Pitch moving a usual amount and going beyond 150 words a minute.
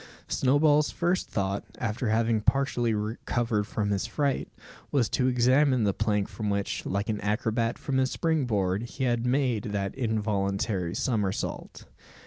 No: average, 4.0 semitones; average, 145 wpm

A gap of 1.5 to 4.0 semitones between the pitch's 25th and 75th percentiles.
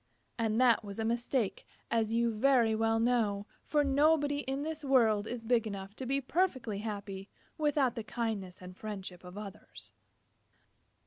No: average, 4.4 semitones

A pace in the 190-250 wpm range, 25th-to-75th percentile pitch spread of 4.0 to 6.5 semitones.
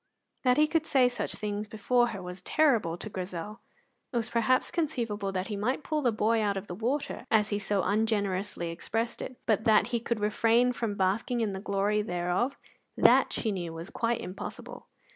No: average, 195 wpm; average, 3.4 semitones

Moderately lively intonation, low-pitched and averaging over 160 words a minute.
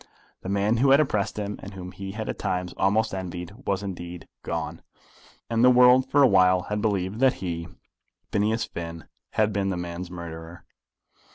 Yes: average, 3.5 semitones; very low, 95 Hz; average, 175 wpm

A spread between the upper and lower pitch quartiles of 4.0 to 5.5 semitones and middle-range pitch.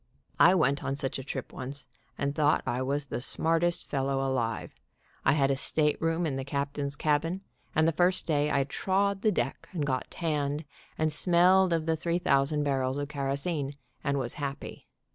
No: average, 3.1 semitones; medium, 145 Hz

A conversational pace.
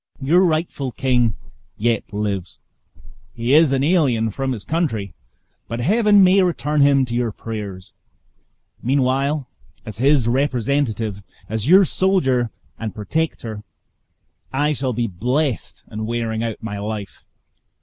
No: slow, 130 wpm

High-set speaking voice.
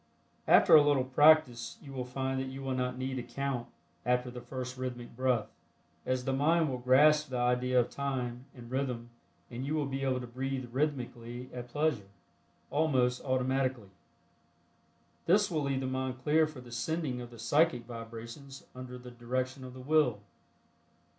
No: low, 130 Hz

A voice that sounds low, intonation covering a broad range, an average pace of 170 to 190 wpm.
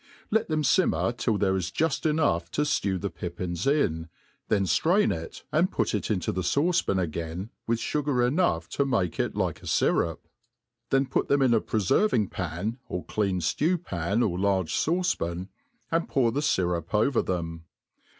Yes: low, 105 Hz; wide, 8.3 semitones; average, 180 wpm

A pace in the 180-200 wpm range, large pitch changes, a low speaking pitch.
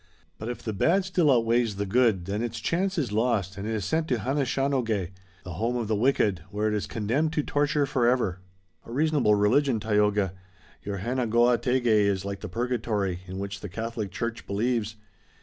No: average, 185 wpm; average, 3.7 semitones; low, 115 Hz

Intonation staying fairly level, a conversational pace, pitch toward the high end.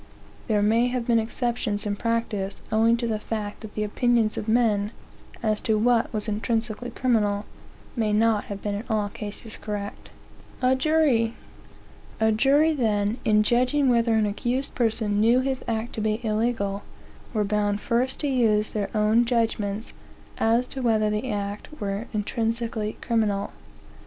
Yes: narrow, 2.2 semitones; average, 150 wpm; high, 220 Hz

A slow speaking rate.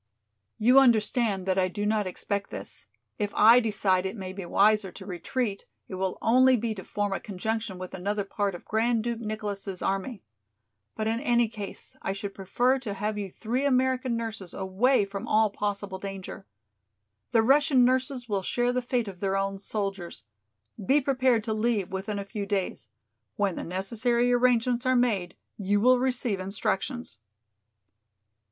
No: average, 170 wpm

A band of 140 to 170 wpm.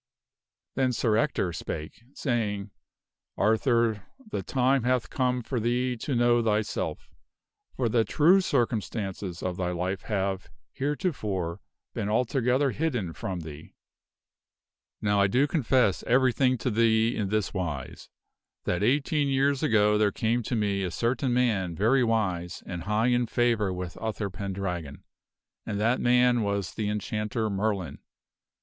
Yes: average, 145 wpm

